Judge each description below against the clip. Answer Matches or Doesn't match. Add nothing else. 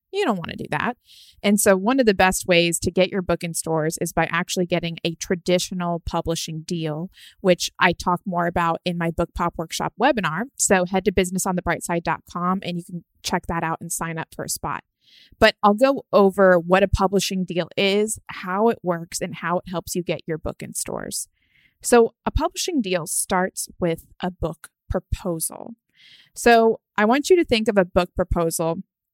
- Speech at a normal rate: Matches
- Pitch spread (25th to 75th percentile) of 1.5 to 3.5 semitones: Matches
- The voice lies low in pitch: Doesn't match